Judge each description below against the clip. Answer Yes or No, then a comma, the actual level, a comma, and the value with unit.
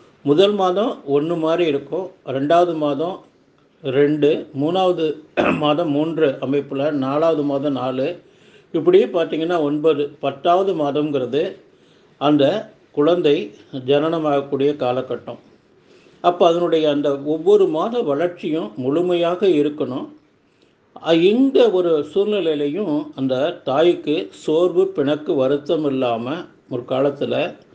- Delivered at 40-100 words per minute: Yes, average, 95 wpm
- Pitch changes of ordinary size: Yes, average, 3.5 semitones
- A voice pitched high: No, medium, 150 Hz